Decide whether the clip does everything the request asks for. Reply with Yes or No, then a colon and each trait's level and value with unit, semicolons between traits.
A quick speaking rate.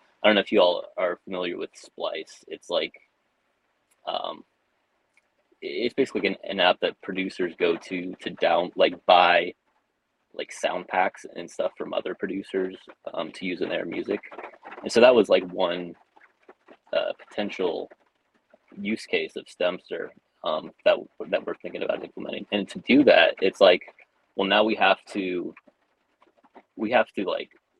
No: average, 160 wpm